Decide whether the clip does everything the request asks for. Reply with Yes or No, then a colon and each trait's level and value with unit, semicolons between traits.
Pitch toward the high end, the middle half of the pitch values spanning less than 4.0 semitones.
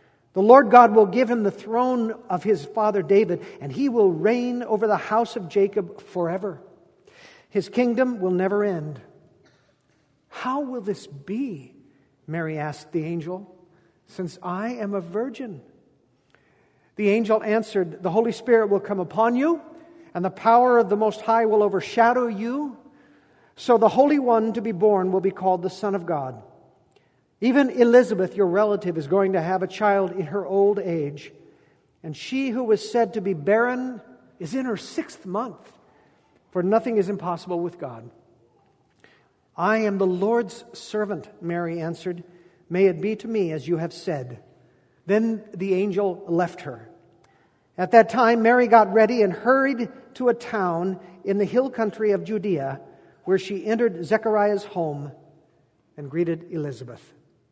No: high, 205 Hz; average, 4.3 semitones